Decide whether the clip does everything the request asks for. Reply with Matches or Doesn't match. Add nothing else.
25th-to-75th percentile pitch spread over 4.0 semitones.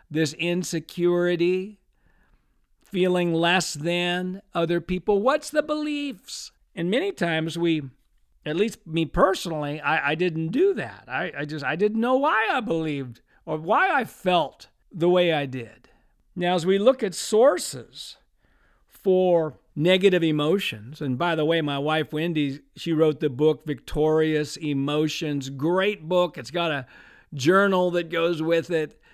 Doesn't match